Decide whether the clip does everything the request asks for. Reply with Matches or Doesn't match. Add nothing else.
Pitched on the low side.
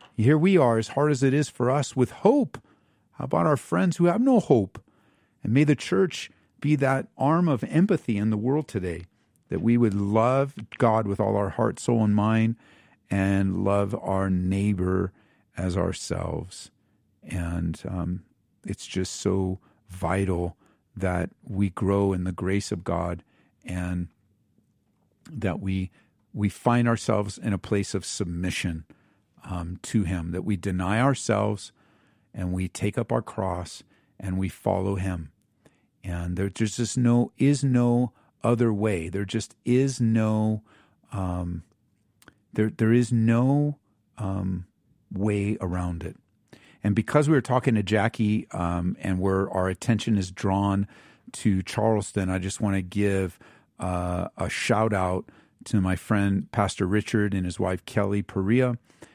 Matches